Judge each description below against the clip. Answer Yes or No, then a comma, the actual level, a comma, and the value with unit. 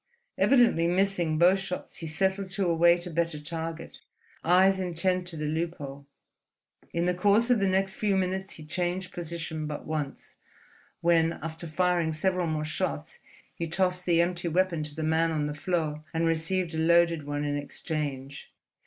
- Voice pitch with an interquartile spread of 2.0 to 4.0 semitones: Yes, narrow, 2.6 semitones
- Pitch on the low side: No, medium, 170 Hz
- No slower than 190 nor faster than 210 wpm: No, average, 170 wpm